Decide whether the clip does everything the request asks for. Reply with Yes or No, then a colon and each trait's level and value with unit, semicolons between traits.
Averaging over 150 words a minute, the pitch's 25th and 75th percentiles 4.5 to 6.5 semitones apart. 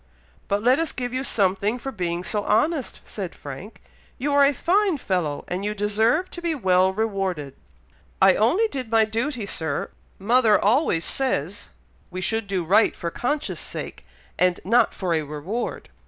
Yes: average, 170 wpm; wide, 5.6 semitones